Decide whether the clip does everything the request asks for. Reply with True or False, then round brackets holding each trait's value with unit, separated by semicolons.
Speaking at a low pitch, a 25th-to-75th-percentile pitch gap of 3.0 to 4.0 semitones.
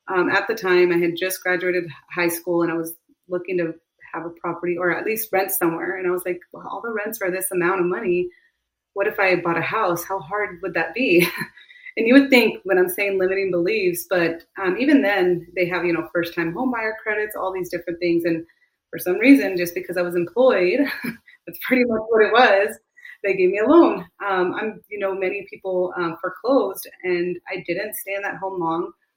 False (185 Hz; 3.6 semitones)